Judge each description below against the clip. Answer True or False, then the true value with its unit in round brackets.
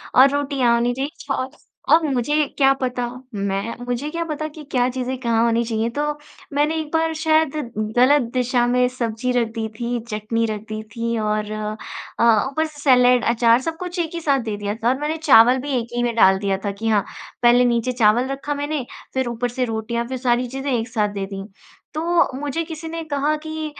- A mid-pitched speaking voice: False (250 Hz)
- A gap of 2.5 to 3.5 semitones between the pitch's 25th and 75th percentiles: False (4.2 semitones)